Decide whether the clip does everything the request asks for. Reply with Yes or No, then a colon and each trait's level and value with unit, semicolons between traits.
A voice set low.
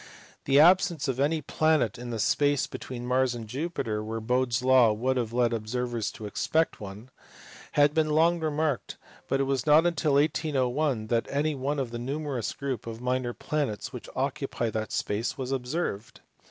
Yes: low, 130 Hz